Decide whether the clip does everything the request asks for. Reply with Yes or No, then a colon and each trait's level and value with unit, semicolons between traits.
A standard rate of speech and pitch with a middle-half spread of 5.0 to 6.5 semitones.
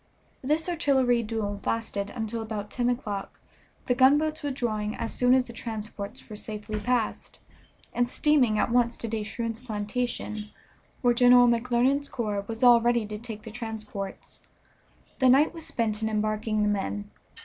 No: average, 160 wpm; average, 2.7 semitones